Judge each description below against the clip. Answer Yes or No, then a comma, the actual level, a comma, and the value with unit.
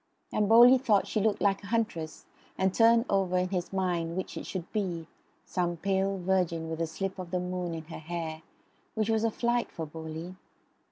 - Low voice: No, medium, 185 Hz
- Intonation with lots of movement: No, average, 3.6 semitones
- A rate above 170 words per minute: Yes, average, 200 wpm